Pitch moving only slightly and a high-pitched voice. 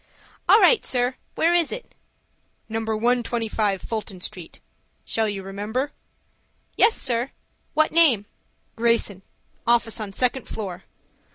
No: average, 3.6 semitones; high, 230 Hz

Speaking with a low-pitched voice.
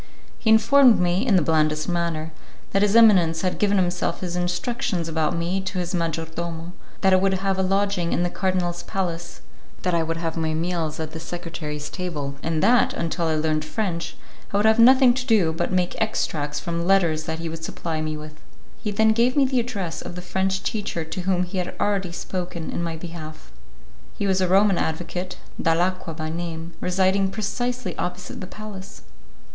No: medium, 175 Hz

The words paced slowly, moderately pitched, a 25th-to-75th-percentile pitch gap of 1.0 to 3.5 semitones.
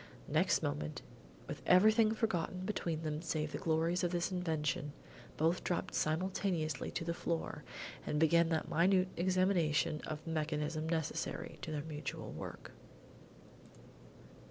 Yes: slow, 130 wpm; medium, 165 Hz; average, 2.8 semitones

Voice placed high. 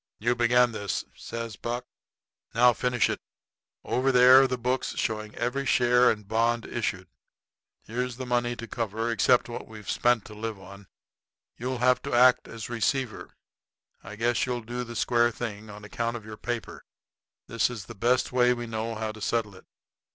No: low, 120 Hz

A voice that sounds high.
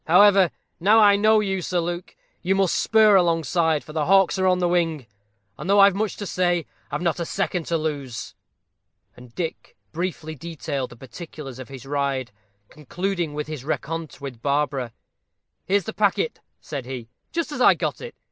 No: medium, 170 Hz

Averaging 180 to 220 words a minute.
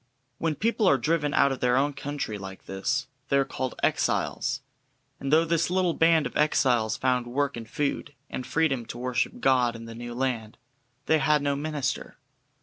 Yes: average, 185 wpm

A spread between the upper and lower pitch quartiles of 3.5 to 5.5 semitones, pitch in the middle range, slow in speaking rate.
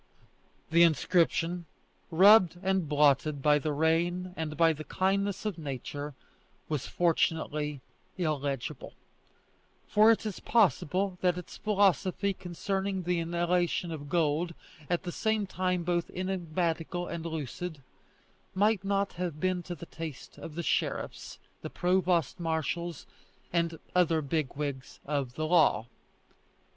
No: average, 3.1 semitones; medium, 170 Hz; slow, 130 wpm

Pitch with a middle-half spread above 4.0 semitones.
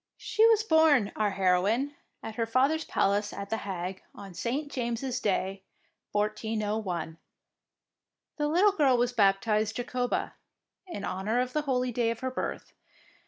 Yes: average, 4.5 semitones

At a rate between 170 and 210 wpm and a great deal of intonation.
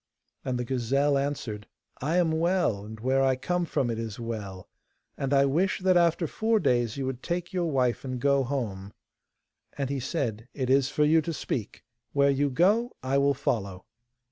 No: average, 190 wpm; average, 4.8 semitones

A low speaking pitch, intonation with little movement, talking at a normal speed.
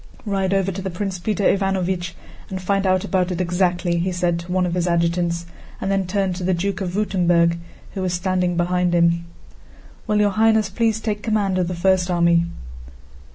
No: medium, 185 Hz; narrow, 1.9 semitones; average, 190 wpm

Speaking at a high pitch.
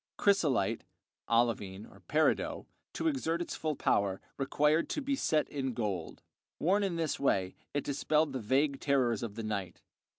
No: medium, 140 Hz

